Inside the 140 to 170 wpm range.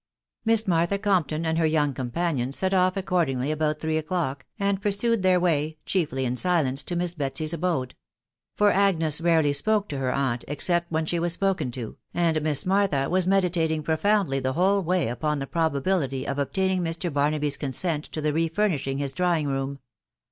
No: average, 180 wpm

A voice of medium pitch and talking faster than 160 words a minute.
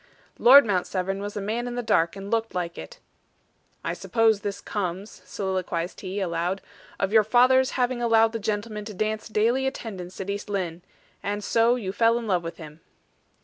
No: high, 205 Hz; average, 190 wpm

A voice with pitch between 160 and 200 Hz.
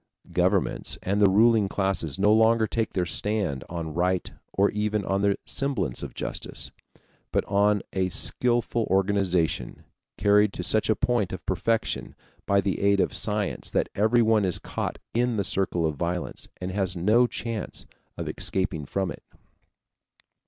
No: low, 100 Hz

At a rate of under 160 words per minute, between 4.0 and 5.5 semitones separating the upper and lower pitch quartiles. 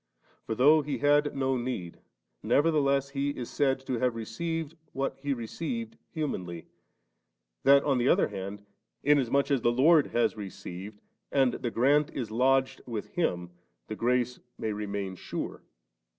Yes: average, 150 wpm; average, 4.4 semitones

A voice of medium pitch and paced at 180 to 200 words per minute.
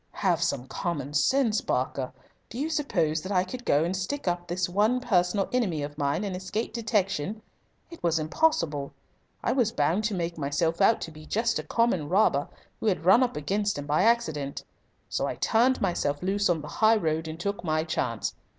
Yes: medium, 180 Hz; average, 195 wpm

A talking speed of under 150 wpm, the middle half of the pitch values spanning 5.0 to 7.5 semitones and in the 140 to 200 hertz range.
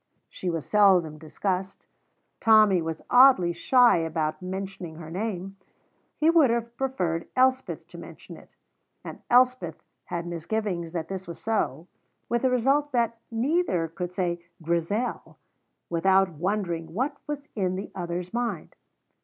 Yes: slow, 135 wpm; wide, 5.6 semitones; high, 190 Hz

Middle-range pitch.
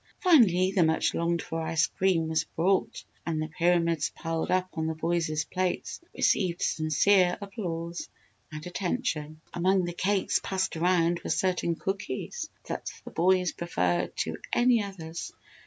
Yes: medium, 175 Hz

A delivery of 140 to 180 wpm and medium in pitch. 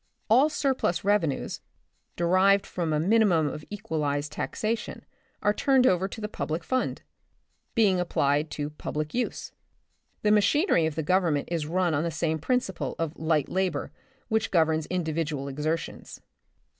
Yes: average, 145 wpm; medium, 170 Hz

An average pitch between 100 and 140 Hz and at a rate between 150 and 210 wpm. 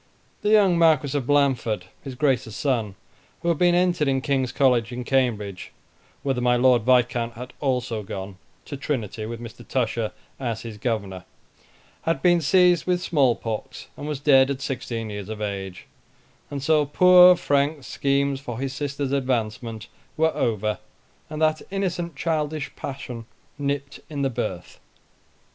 Yes: low, 135 Hz; average, 155 wpm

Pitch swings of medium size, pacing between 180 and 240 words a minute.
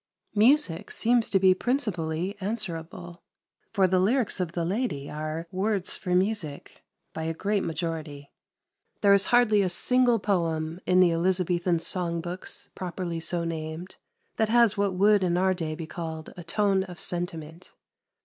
No: average, 3.5 semitones; average, 155 wpm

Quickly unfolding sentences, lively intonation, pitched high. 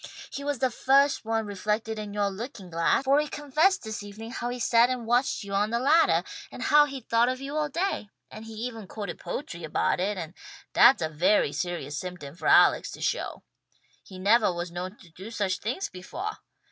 Yes: fast, 210 wpm; wide, 5.8 semitones; high, 220 Hz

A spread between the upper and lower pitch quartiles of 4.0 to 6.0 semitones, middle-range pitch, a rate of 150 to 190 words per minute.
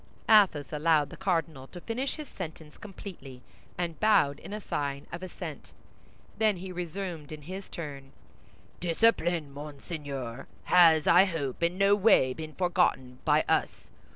No: average, 4.7 semitones; medium, 165 Hz; average, 140 wpm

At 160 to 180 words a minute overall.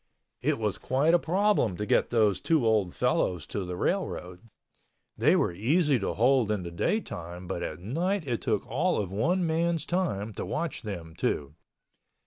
Yes: average, 175 wpm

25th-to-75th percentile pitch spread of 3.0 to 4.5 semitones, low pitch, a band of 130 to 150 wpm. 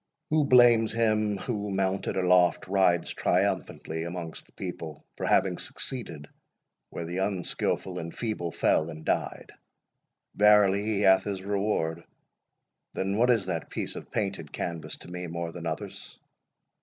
Yes: average, 3.6 semitones; very low, 95 Hz; average, 145 wpm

